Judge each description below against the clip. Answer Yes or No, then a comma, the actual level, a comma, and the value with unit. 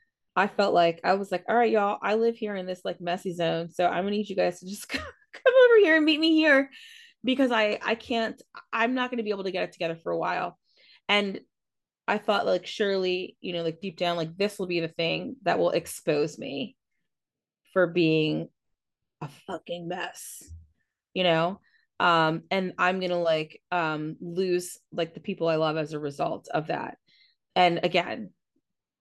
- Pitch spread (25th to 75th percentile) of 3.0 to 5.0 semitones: Yes, average, 4.2 semitones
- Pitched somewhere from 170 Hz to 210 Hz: Yes, medium, 185 Hz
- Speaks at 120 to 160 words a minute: No, average, 200 wpm